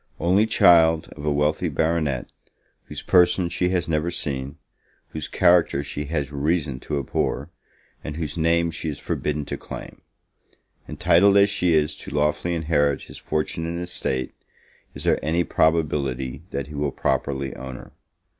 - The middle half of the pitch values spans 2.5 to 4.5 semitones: Yes, average, 3.0 semitones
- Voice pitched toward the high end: No, very low, 80 Hz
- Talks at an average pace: Yes, average, 155 wpm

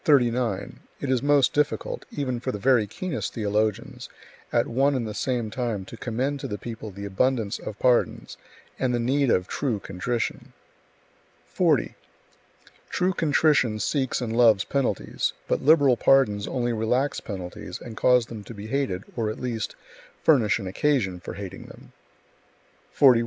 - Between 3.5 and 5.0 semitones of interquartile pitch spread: Yes, average, 4.1 semitones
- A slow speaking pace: No, average, 155 wpm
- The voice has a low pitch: Yes, low, 120 Hz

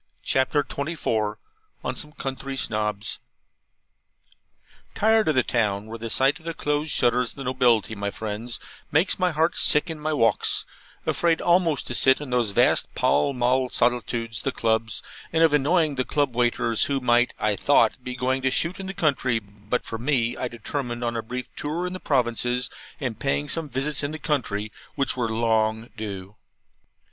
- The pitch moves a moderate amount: Yes, average, 4.3 semitones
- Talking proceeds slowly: No, average, 180 wpm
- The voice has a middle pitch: No, low, 125 Hz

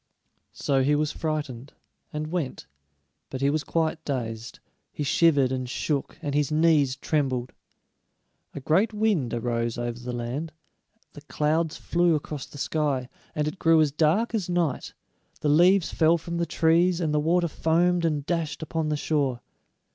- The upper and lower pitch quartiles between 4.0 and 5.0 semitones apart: No, average, 3.4 semitones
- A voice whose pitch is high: No, medium, 150 Hz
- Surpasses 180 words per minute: No, average, 160 wpm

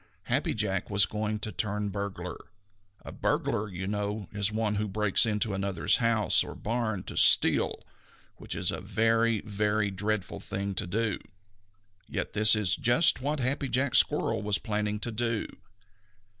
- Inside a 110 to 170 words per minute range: Yes, average, 155 wpm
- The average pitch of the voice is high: No, low, 105 Hz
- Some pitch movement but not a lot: No, narrow, 2.0 semitones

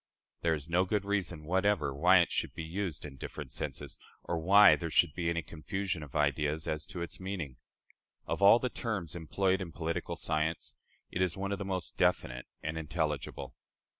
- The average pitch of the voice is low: Yes, very low, 85 Hz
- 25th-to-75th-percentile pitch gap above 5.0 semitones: No, average, 3.6 semitones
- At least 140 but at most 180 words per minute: No, average, 190 wpm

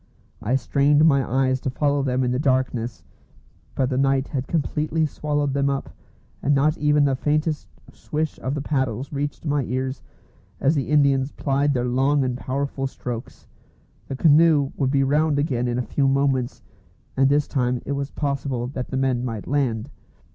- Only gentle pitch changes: Yes, narrow, 1.9 semitones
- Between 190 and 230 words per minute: No, average, 175 wpm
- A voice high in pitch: No, low, 135 Hz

